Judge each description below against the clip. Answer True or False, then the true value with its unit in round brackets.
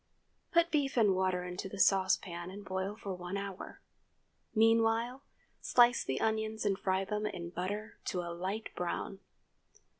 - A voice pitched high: True (200 Hz)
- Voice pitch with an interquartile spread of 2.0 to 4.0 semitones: True (3.0 semitones)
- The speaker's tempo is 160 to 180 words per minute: False (150 wpm)